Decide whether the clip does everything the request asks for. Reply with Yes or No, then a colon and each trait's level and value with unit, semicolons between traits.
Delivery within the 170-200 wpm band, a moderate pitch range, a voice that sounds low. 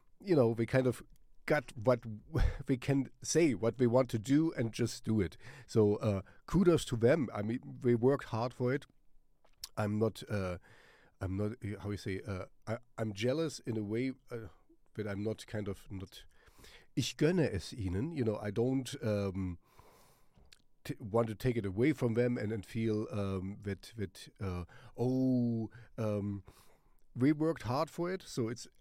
Yes: average, 180 wpm; average, 3.9 semitones; low, 115 Hz